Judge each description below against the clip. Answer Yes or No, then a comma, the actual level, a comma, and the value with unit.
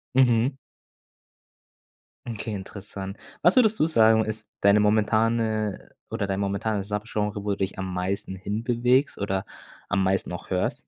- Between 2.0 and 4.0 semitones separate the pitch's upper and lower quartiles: Yes, narrow, 2.6 semitones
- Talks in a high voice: No, low, 105 Hz